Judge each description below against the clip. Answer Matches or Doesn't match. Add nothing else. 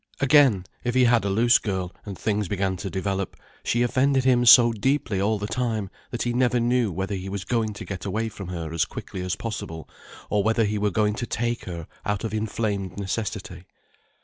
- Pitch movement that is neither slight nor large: Matches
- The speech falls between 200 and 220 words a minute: Matches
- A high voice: Doesn't match